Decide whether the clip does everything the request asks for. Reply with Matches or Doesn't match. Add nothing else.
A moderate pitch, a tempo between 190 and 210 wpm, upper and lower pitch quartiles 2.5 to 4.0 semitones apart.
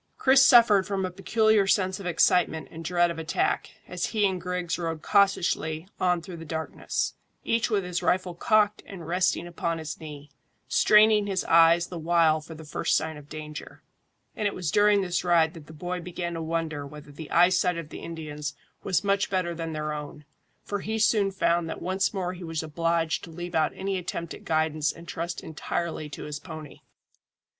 Matches